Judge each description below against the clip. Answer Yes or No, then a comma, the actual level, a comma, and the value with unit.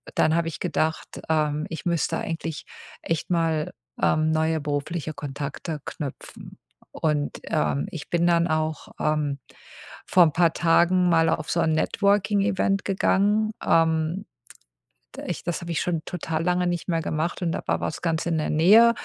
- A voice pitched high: No, medium, 165 Hz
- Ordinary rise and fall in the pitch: No, narrow, 2.0 semitones